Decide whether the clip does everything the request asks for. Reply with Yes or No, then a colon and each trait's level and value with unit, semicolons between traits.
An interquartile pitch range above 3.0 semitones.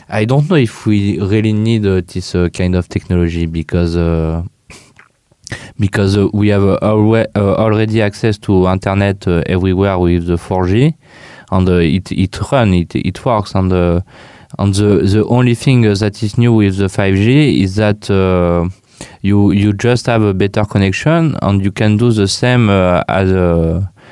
No: average, 2.7 semitones